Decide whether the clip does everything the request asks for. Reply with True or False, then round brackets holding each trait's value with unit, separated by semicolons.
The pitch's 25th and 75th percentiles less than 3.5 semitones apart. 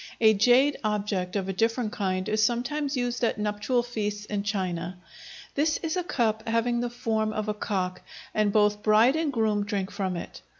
True (2.9 semitones)